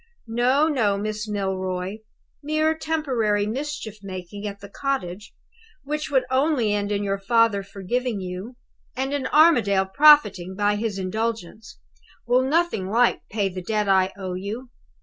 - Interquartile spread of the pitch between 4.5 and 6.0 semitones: Yes, average, 4.9 semitones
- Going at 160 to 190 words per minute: No, average, 145 wpm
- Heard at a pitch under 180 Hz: No, high, 215 Hz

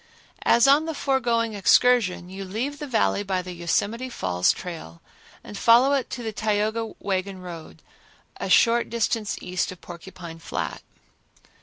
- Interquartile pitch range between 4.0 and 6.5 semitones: Yes, average, 4.6 semitones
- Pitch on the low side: No, high, 210 Hz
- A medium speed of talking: Yes, average, 150 wpm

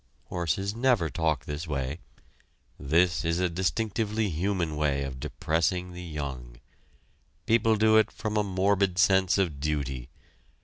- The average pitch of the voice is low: Yes, very low, 90 Hz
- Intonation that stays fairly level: No, average, 4.8 semitones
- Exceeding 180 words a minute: No, slow, 135 wpm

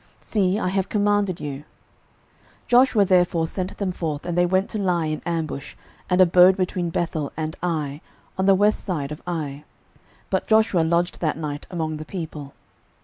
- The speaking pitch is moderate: Yes, medium, 175 Hz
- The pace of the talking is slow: No, average, 175 wpm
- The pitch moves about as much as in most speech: Yes, average, 3.4 semitones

